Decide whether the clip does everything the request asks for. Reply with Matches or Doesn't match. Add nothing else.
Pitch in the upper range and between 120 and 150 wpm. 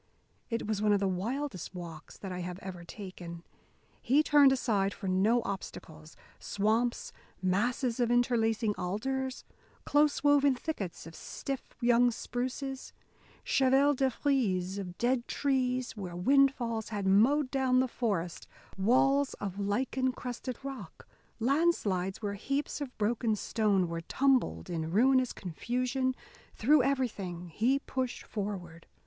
Matches